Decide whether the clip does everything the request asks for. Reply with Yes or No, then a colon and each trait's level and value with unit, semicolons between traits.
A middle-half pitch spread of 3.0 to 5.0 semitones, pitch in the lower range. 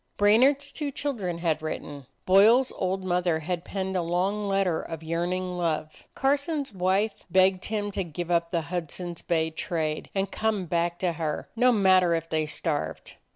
No: average, 3.4 semitones; medium, 180 Hz